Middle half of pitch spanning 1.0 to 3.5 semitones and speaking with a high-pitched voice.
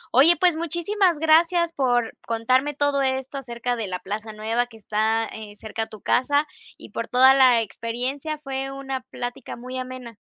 No: average, 3.9 semitones; very high, 255 Hz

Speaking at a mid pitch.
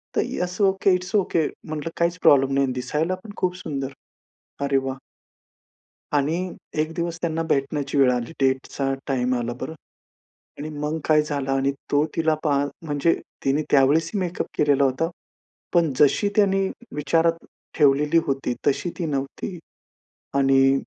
Yes: medium, 150 Hz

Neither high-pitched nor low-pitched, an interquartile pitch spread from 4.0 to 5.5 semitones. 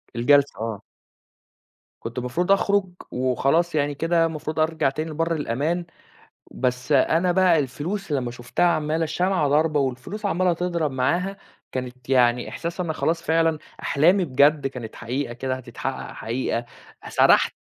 Yes: medium, 150 Hz; average, 4.8 semitones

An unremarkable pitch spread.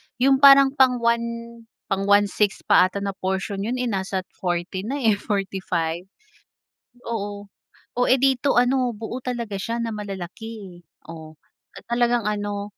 Yes: average, 3.7 semitones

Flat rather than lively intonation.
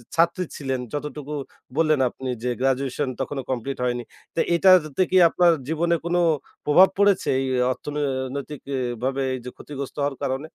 No: average, 4.0 semitones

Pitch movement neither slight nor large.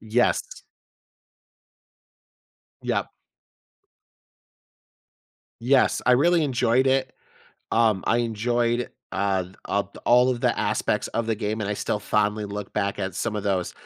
Yes: average, 3.2 semitones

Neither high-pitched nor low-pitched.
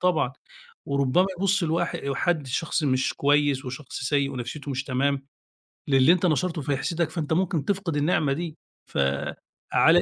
Yes: medium, 145 Hz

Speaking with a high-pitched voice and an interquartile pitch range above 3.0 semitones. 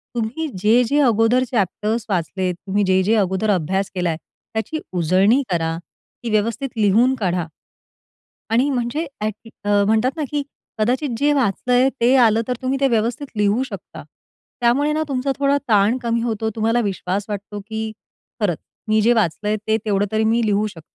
Yes: high, 220 Hz; average, 3.6 semitones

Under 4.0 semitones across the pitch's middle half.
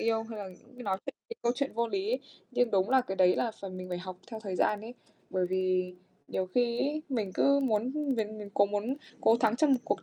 No: average, 4.7 semitones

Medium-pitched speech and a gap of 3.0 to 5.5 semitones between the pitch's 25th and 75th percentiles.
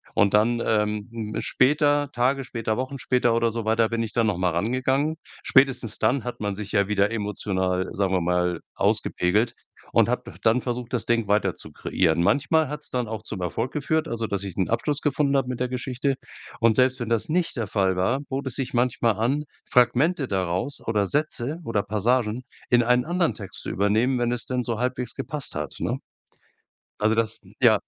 No: low, 115 Hz; average, 3.8 semitones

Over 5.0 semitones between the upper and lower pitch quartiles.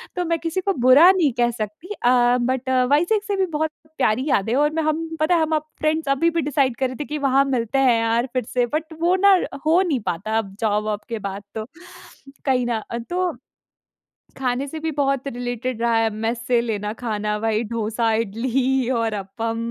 Yes: wide, 5.4 semitones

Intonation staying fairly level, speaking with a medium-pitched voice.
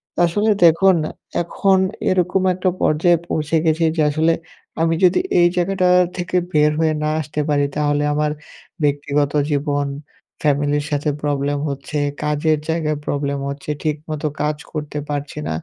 Yes: narrow, 2.3 semitones; medium, 150 Hz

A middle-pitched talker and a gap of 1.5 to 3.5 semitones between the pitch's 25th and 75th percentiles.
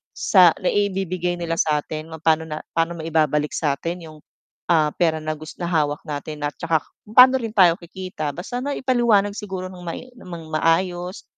Yes: medium, 170 Hz; average, 3.2 semitones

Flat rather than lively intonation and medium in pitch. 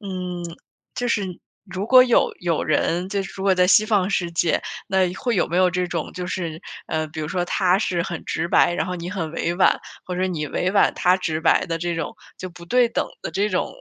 Yes: narrow, 2.1 semitones; medium, 180 Hz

